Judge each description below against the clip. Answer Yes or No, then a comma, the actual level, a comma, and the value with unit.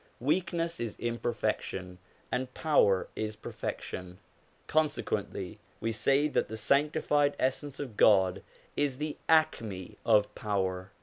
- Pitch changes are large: Yes, wide, 6.5 semitones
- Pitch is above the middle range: No, low, 120 Hz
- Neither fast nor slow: No, slow, 115 wpm